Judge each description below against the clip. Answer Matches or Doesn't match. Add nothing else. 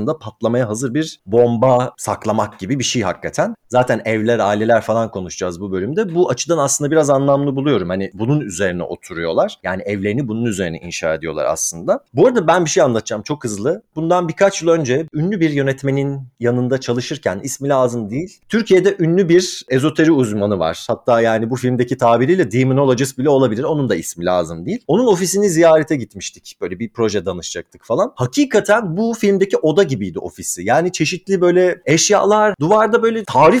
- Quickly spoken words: Matches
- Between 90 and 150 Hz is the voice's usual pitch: Matches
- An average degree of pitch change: Doesn't match